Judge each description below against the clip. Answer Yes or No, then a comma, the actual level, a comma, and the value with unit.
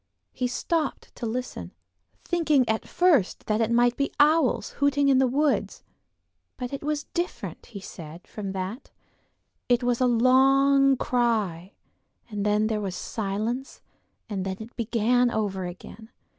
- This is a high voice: Yes, high, 240 Hz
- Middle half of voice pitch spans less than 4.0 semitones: No, average, 4.5 semitones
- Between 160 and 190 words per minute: No, average, 145 wpm